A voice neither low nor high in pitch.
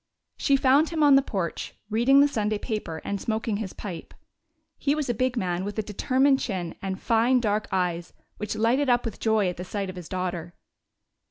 No: high, 215 Hz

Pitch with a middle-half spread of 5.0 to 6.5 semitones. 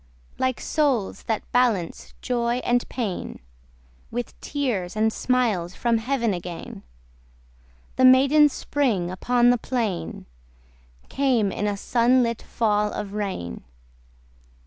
No: average, 3.7 semitones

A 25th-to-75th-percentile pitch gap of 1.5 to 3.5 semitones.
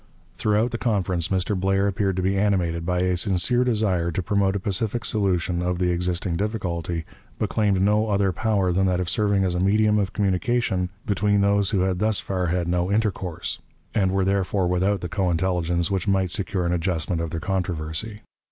Yes: narrow, 2.4 semitones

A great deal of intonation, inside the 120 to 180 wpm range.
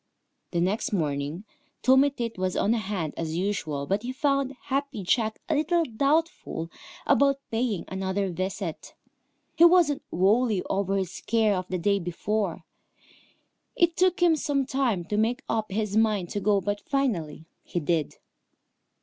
Yes: wide, 6.6 semitones; average, 150 wpm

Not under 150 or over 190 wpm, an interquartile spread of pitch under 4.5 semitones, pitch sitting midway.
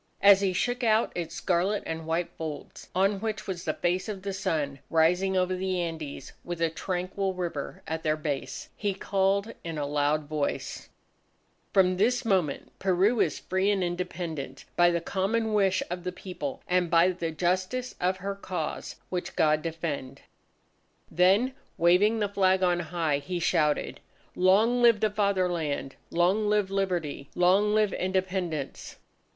Yes: average, 155 wpm; average, 3.1 semitones; medium, 180 Hz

